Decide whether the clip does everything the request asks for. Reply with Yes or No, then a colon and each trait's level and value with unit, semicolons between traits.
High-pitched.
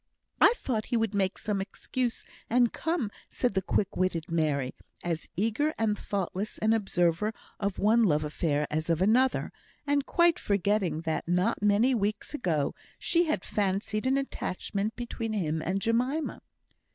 Yes: high, 210 Hz